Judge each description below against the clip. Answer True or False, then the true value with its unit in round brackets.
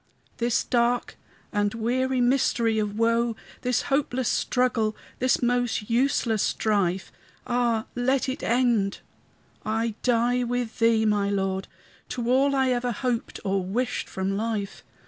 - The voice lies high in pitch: True (235 Hz)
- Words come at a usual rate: False (130 wpm)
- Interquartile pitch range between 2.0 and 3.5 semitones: True (2.5 semitones)